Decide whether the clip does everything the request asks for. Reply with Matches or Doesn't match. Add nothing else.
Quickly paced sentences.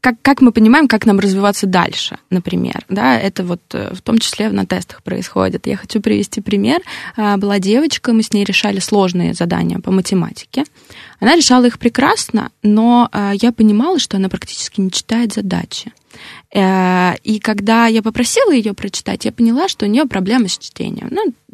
Matches